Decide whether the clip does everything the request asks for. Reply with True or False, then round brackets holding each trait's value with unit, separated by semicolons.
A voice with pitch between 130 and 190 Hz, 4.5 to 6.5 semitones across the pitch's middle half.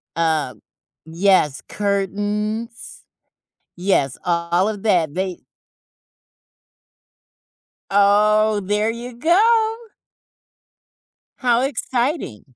False (205 Hz; 4.8 semitones)